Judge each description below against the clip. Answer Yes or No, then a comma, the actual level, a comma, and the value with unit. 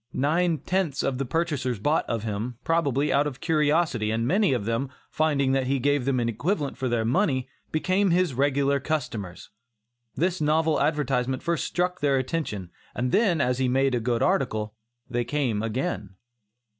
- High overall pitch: No, low, 135 Hz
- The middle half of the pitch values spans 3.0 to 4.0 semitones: No, average, 4.6 semitones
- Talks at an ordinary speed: Yes, average, 170 wpm